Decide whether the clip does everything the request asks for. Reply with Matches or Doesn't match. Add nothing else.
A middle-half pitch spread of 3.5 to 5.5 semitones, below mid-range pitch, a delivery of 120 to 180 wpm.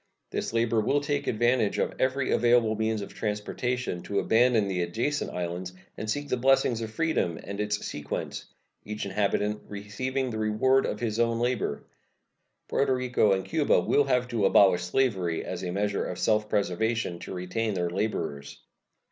Matches